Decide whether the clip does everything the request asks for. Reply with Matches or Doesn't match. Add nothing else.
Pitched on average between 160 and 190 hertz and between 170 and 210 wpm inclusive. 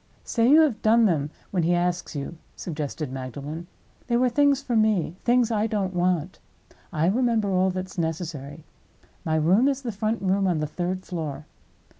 Matches